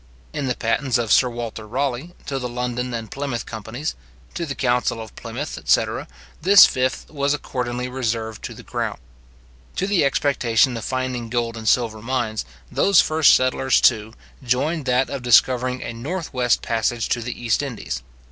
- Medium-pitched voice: No, low, 125 Hz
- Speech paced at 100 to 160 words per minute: No, average, 170 wpm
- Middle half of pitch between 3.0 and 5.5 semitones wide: No, narrow, 2.6 semitones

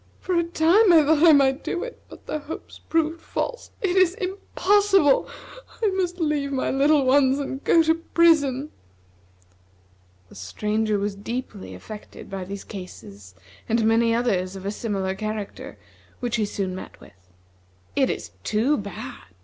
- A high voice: Yes, very high, 265 Hz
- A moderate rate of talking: Yes, average, 155 wpm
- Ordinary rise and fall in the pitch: No, wide, 8.1 semitones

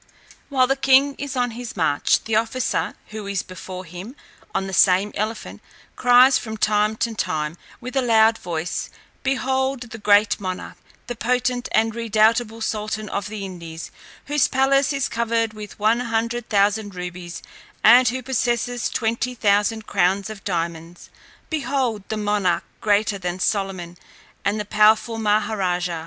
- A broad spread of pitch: No, average, 3.6 semitones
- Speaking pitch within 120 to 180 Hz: No, high, 215 Hz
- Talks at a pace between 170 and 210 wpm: No, average, 150 wpm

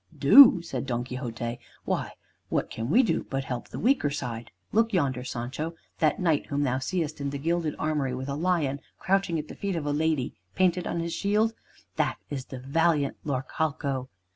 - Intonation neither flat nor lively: Yes, average, 4.4 semitones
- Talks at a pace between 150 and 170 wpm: No, average, 190 wpm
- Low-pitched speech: No, medium, 145 Hz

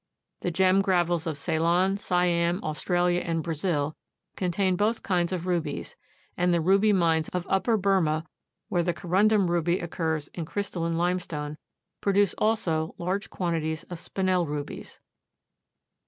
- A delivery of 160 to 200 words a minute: No, average, 140 wpm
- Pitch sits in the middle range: Yes, medium, 175 Hz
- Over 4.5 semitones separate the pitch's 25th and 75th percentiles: No, narrow, 2.4 semitones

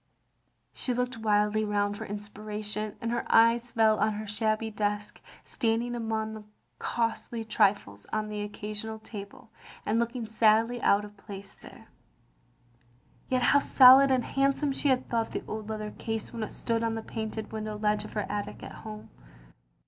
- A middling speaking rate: Yes, average, 165 wpm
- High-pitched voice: Yes, high, 220 Hz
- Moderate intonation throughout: No, narrow, 1.7 semitones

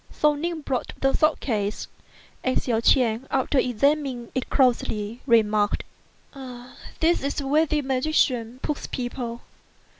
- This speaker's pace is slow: Yes, slow, 125 wpm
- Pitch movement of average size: Yes, average, 3.8 semitones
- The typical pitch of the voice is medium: No, very high, 255 Hz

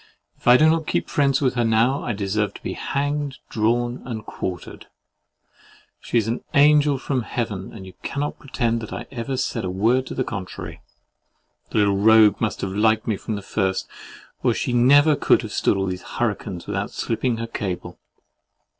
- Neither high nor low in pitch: No, low, 115 Hz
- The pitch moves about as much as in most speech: Yes, average, 4.3 semitones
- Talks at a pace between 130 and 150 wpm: No, average, 185 wpm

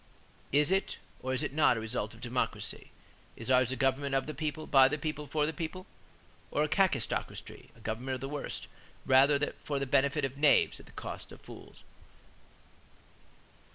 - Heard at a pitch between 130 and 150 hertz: Yes, medium, 140 Hz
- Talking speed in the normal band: Yes, average, 185 wpm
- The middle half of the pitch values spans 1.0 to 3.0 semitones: Yes, narrow, 2.6 semitones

